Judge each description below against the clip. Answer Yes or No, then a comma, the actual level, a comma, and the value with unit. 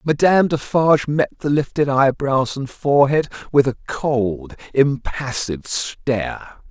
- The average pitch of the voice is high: No, low, 135 Hz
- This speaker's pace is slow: Yes, slow, 115 wpm